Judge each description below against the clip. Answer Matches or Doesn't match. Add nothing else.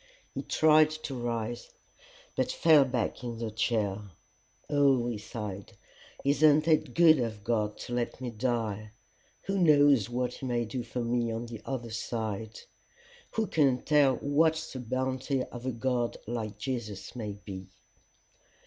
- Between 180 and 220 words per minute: Doesn't match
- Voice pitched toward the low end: Matches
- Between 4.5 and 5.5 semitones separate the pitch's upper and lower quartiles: Doesn't match